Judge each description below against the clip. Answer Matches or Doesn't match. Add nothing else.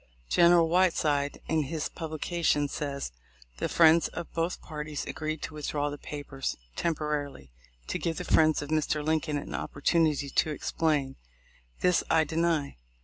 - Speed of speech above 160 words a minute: Doesn't match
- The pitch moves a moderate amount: Doesn't match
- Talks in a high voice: Doesn't match